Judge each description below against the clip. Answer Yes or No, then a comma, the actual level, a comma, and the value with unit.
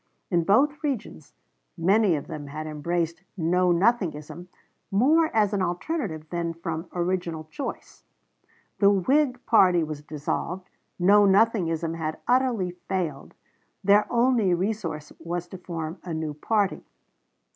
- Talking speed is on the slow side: Yes, slow, 125 wpm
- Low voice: No, medium, 180 Hz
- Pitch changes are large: No, average, 4.3 semitones